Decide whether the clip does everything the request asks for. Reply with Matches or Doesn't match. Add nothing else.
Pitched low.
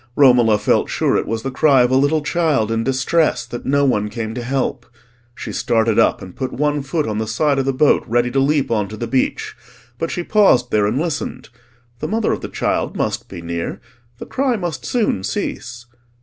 Matches